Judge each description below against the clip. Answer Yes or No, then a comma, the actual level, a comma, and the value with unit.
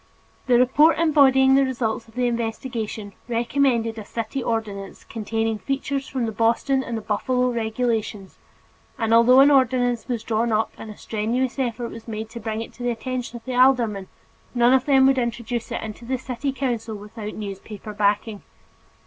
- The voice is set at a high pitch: Yes, high, 235 Hz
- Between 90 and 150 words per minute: No, average, 175 wpm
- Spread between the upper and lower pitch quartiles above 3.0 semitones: No, average, 2.7 semitones